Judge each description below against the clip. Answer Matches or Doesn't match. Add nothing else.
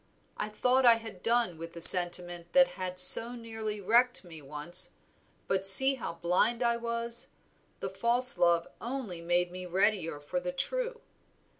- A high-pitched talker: Matches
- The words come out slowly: Doesn't match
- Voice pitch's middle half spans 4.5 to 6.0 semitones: Matches